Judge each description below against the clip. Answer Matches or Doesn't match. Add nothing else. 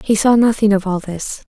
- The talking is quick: Matches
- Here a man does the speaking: Doesn't match